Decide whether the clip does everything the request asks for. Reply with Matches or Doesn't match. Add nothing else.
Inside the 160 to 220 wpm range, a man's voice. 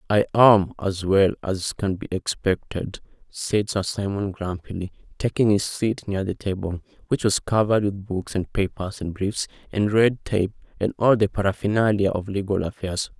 Matches